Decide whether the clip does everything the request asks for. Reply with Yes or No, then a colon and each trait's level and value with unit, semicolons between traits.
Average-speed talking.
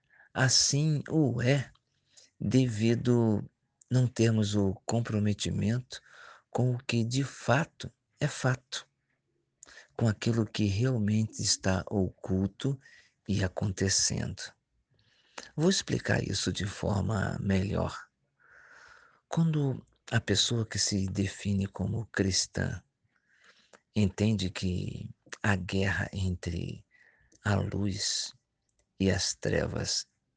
No: slow, 95 wpm